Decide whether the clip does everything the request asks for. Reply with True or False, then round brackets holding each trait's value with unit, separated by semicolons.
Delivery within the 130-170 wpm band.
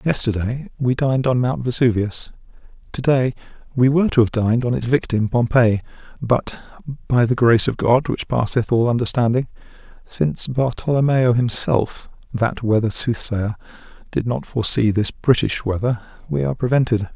True (145 wpm)